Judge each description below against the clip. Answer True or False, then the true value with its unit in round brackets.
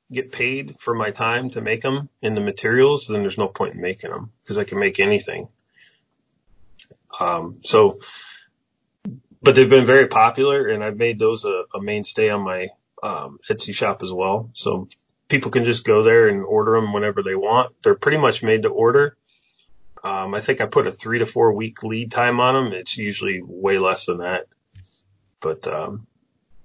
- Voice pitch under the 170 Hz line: True (135 Hz)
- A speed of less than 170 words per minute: False (190 wpm)